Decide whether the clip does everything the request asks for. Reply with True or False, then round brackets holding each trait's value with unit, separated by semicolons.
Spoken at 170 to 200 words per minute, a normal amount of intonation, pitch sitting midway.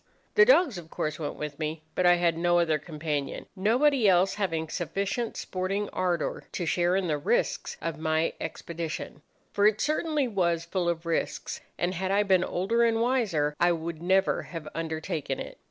True (180 wpm; 3.7 semitones; 175 Hz)